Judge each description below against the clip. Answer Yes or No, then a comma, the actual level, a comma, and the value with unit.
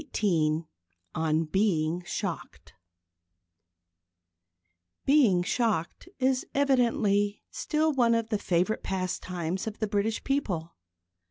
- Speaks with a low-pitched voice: No, high, 205 Hz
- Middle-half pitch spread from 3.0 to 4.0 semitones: No, wide, 5.6 semitones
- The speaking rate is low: Yes, slow, 95 wpm